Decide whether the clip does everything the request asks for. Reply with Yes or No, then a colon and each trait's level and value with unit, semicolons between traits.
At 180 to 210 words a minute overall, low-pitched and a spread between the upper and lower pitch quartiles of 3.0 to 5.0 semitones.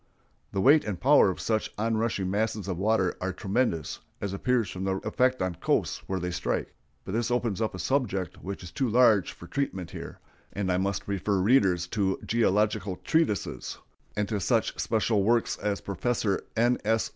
Yes: average, 185 wpm; low, 105 Hz; average, 3.4 semitones